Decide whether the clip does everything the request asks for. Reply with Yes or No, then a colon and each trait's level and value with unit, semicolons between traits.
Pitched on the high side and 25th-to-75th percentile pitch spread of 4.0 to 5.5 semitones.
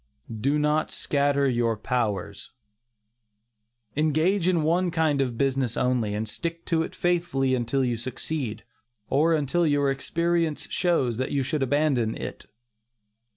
No: medium, 140 Hz; average, 4.4 semitones